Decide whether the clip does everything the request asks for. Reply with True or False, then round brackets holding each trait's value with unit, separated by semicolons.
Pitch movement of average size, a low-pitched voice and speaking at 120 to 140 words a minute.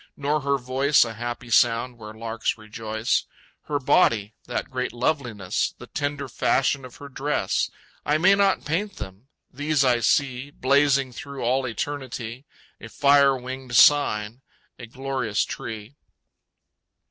True (3.6 semitones; 130 Hz; 135 wpm)